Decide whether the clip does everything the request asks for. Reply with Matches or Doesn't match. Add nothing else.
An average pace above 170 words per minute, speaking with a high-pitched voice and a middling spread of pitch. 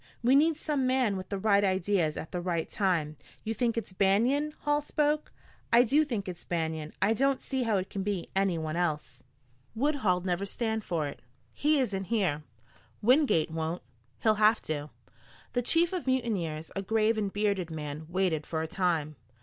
Doesn't match